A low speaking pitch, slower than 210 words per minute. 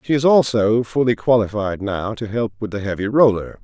Yes: low, 110 Hz; average, 200 wpm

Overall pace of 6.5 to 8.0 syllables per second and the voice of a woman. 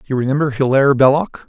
No: 6.8 syllables/s; male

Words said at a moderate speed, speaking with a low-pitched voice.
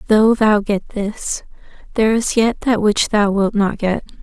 No: average, 185 wpm; high, 210 Hz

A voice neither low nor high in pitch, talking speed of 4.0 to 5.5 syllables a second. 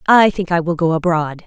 Yes: medium, 170 Hz; 5.4 syllables/s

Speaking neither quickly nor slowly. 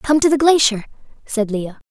Yes: average, 190 wpm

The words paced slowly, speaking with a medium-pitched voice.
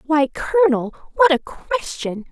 No: slow, 130 wpm; very high, 310 Hz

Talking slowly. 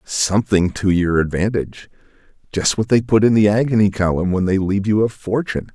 No: average, 190 wpm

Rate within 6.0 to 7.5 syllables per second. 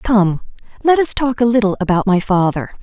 No: 5.2 syllables/s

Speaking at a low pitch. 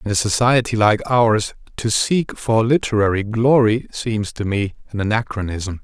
Yes: low, 110 Hz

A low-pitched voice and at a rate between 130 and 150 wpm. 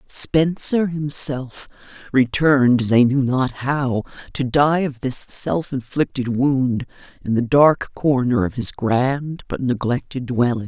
Yes: low, 130 Hz; slow, 135 wpm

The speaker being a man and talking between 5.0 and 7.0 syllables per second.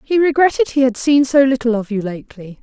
No: female; 6.0 syllables/s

